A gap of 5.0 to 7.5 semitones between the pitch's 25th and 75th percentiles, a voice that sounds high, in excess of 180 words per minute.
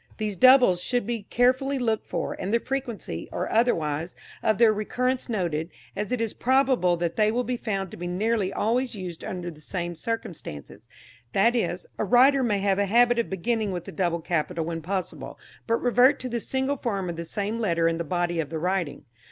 Yes: wide, 5.5 semitones; high, 205 Hz; average, 200 wpm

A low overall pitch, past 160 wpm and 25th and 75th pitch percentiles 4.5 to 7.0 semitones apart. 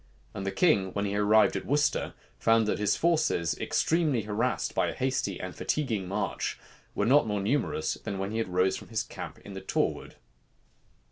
Yes: low, 105 Hz; average, 185 wpm; average, 4.9 semitones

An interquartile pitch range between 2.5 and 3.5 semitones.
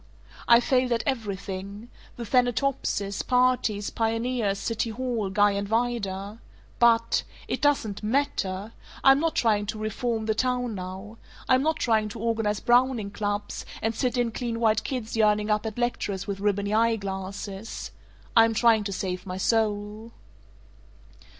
Yes: average, 2.8 semitones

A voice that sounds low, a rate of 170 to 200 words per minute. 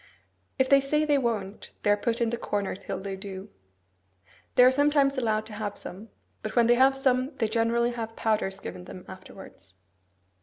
No: high, 225 Hz; average, 190 wpm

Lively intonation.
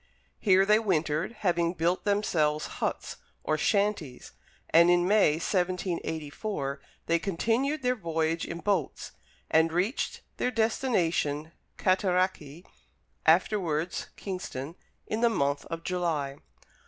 No: average, 4.2 semitones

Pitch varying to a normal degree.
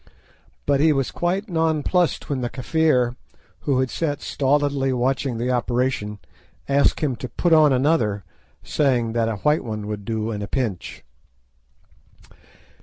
Yes: average, 4.1 semitones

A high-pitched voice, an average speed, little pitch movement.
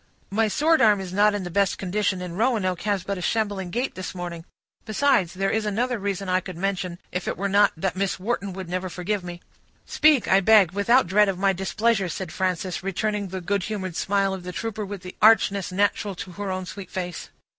No: high, 195 Hz; fast, 220 wpm; narrow, 2.3 semitones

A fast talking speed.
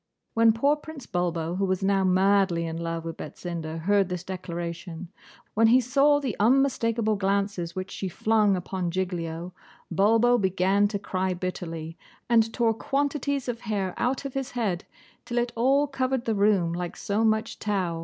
No: average, 165 wpm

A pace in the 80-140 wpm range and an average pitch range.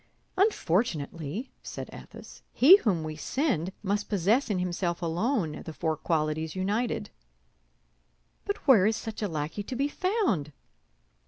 No: slow, 135 wpm; wide, 7.3 semitones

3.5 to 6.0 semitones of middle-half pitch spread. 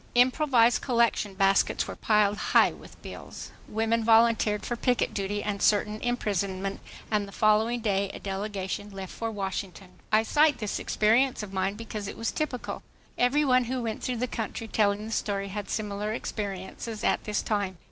No: narrow, 2.6 semitones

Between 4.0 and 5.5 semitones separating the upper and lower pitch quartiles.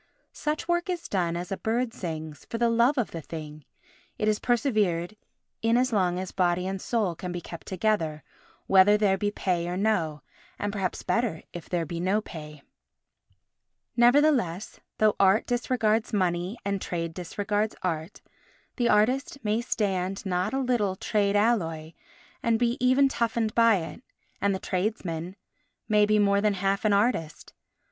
Yes: average, 4.4 semitones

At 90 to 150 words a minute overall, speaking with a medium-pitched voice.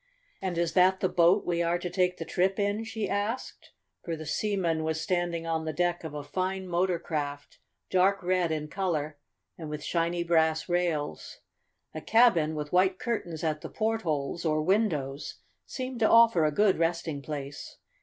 No: average, 175 wpm; medium, 170 Hz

